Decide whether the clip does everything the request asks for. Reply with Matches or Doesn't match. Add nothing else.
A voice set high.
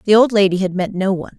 Matches